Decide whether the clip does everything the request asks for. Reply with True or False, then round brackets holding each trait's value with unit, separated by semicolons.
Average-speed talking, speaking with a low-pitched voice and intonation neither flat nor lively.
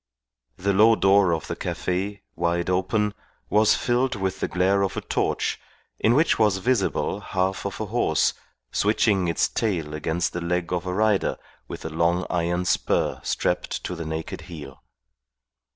True (165 wpm; 95 Hz; 3.3 semitones)